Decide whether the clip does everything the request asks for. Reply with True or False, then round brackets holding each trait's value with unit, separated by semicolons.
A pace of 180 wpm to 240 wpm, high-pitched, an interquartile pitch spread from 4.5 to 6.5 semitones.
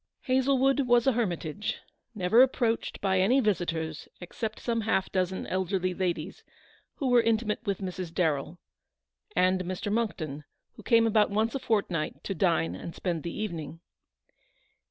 False (150 wpm; 195 Hz; 4.8 semitones)